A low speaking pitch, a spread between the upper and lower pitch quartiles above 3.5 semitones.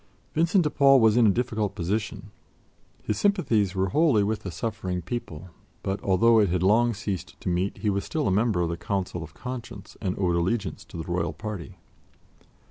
Yes: low, 100 Hz; average, 4.2 semitones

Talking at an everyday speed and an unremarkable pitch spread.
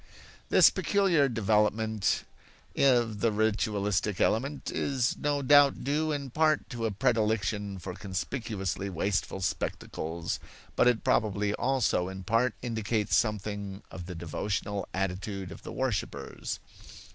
No: slow, 120 wpm; average, 4.1 semitones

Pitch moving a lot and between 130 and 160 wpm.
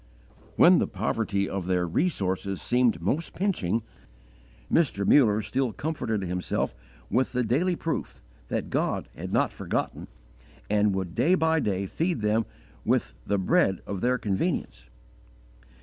Yes: wide, 6.0 semitones; slow, 135 wpm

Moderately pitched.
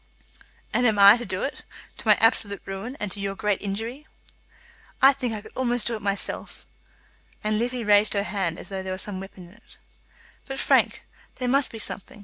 No: high, 210 Hz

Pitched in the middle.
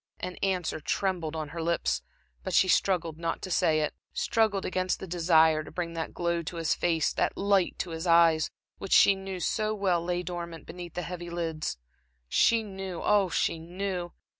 Yes: medium, 175 Hz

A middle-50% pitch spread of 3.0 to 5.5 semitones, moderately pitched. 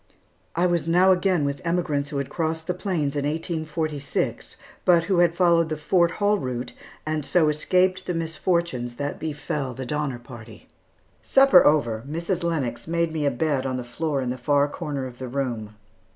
Yes: average, 3.9 semitones; medium, 155 Hz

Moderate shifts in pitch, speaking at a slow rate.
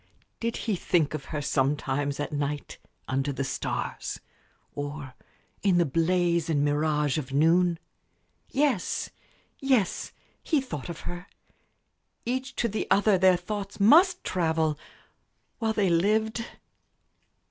No: wide, 6.3 semitones; slow, 125 wpm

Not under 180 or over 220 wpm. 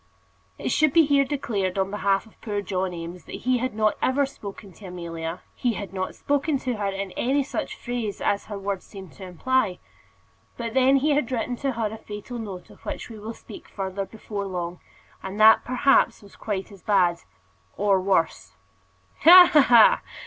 Yes: average, 190 wpm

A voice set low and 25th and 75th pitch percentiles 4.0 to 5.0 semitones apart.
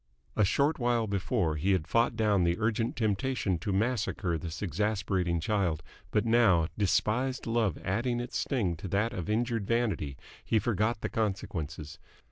Yes: low, 105 Hz; average, 4.4 semitones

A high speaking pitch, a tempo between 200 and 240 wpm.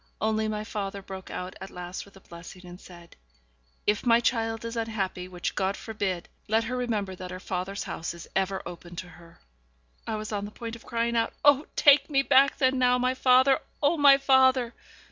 Yes: high, 215 Hz; fast, 205 wpm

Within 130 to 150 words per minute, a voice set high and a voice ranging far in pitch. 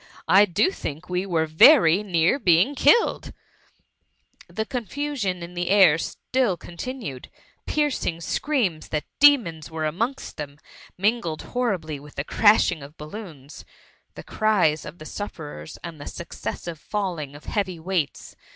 No: average, 140 wpm; medium, 180 Hz; wide, 5.7 semitones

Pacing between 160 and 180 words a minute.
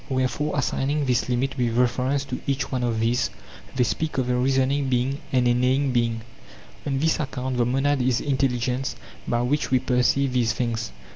No: average, 190 wpm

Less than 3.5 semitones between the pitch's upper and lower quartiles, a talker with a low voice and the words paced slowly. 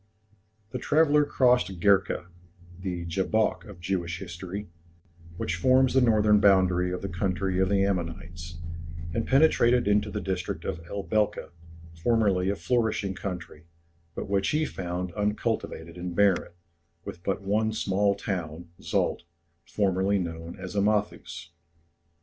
Yes: average, 3.1 semitones; very low, 95 Hz; slow, 130 wpm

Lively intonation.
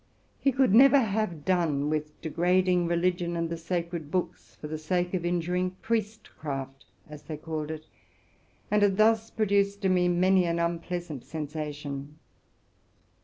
No: average, 3.4 semitones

